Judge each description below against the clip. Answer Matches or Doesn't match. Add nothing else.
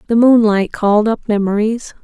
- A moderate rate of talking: Matches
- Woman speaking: Matches